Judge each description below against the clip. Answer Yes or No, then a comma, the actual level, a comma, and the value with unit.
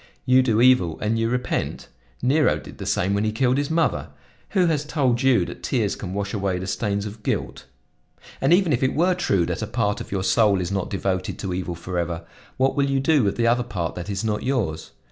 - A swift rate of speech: Yes, fast, 230 wpm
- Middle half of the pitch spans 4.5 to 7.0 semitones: Yes, wide, 5.6 semitones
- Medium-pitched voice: No, low, 110 Hz